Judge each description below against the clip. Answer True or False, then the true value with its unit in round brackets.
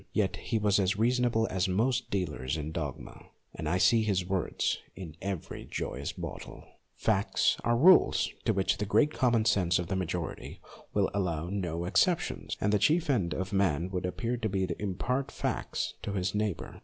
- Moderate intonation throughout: True (4.1 semitones)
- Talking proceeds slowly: False (185 wpm)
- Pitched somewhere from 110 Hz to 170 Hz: False (95 Hz)